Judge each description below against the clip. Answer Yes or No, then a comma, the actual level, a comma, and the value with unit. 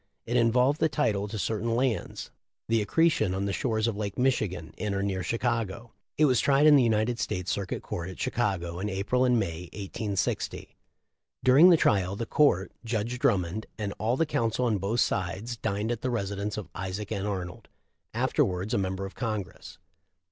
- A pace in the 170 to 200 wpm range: Yes, average, 190 wpm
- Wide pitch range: No, average, 3.7 semitones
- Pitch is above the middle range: No, low, 110 Hz